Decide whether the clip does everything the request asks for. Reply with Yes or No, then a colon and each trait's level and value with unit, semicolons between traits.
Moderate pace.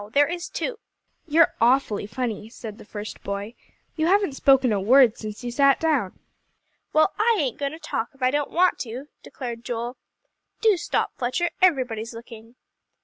Yes: average, 170 wpm